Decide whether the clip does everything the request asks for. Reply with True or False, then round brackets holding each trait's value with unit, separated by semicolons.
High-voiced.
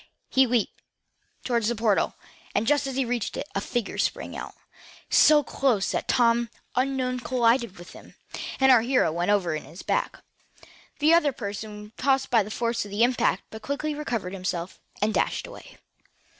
True (235 Hz)